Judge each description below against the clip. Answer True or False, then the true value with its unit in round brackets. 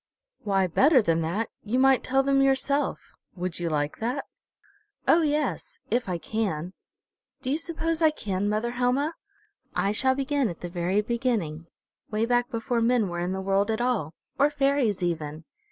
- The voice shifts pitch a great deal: True (6.6 semitones)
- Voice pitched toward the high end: True (230 Hz)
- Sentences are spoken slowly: False (170 wpm)